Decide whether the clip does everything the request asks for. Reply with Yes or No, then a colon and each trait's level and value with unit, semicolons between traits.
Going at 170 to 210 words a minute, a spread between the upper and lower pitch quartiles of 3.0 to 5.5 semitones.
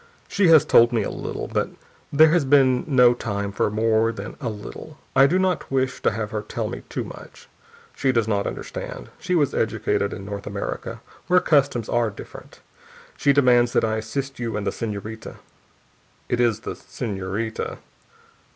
Yes: average, 180 wpm; average, 4.4 semitones